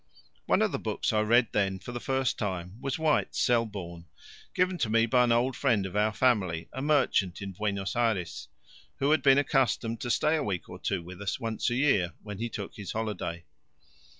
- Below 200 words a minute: No, fast, 205 wpm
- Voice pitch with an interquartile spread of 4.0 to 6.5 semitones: Yes, average, 4.8 semitones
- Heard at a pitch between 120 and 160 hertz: No, low, 110 Hz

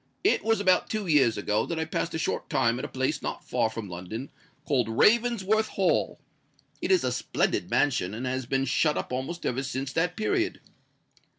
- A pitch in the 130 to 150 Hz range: Yes, medium, 140 Hz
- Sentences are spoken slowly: No, average, 195 wpm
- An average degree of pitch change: No, wide, 7.6 semitones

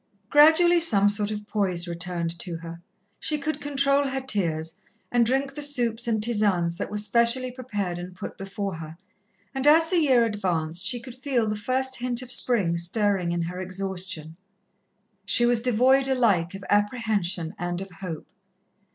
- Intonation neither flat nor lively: No, wide, 6.3 semitones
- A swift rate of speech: No, average, 170 wpm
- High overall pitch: Yes, high, 210 Hz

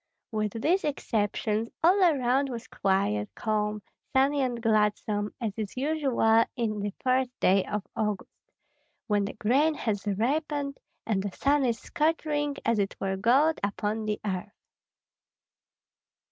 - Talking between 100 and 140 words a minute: Yes, slow, 135 wpm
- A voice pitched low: No, high, 225 Hz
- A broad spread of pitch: No, average, 5.0 semitones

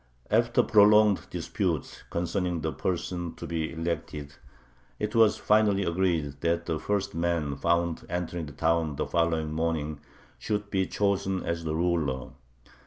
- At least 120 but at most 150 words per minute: Yes, average, 140 wpm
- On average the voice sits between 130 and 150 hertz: No, very low, 85 Hz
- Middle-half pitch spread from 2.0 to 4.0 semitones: Yes, average, 3.4 semitones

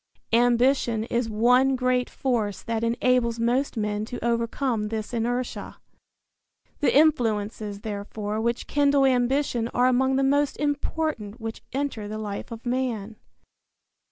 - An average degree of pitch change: Yes, average, 3.0 semitones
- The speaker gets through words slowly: Yes, slow, 130 wpm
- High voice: Yes, high, 240 Hz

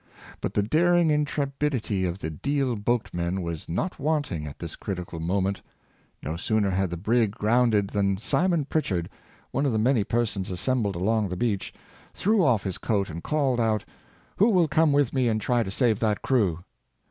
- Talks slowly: No, average, 180 wpm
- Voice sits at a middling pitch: No, low, 110 Hz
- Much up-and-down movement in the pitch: Yes, wide, 6.3 semitones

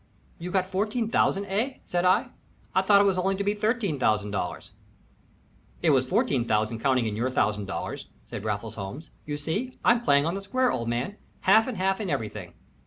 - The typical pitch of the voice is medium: Yes, medium, 180 Hz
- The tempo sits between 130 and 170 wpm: No, average, 185 wpm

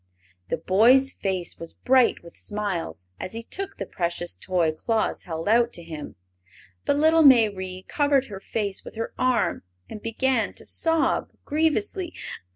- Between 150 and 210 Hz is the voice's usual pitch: No, high, 220 Hz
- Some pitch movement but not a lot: No, wide, 6.4 semitones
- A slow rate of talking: No, average, 155 wpm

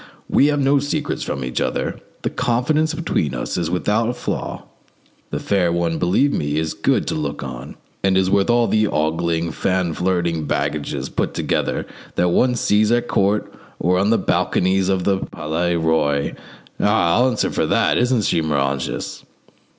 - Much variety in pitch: Yes, wide, 6.1 semitones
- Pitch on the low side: Yes, very low, 90 Hz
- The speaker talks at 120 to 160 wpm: No, average, 175 wpm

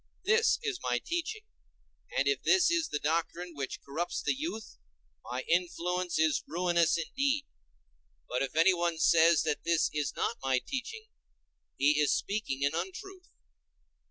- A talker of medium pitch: Yes, medium, 175 Hz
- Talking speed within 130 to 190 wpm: Yes, average, 145 wpm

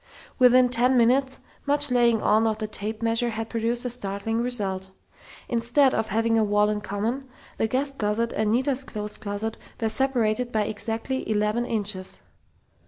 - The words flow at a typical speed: Yes, average, 165 wpm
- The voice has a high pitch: Yes, high, 225 Hz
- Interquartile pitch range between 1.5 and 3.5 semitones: Yes, average, 2.7 semitones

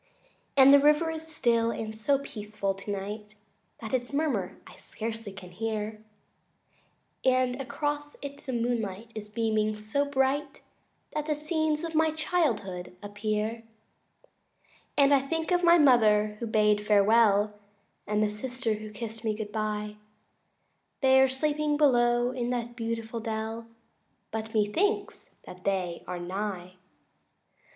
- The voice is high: Yes, high, 230 Hz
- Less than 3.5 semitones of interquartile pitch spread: No, average, 4.8 semitones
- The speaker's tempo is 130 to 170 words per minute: Yes, average, 145 wpm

